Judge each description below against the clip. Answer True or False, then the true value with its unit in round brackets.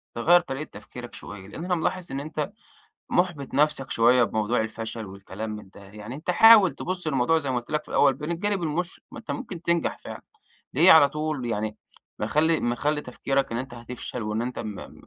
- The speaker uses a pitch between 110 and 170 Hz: True (135 Hz)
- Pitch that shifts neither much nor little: False (5.8 semitones)